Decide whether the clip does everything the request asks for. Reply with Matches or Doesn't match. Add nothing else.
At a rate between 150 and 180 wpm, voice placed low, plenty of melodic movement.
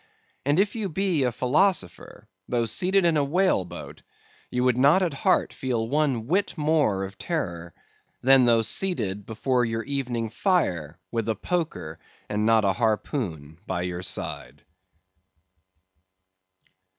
Doesn't match